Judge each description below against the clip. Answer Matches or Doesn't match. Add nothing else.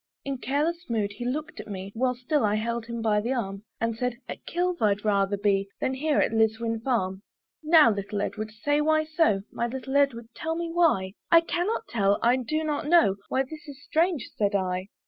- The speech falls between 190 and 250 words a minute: Matches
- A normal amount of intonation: Doesn't match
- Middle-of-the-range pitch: Doesn't match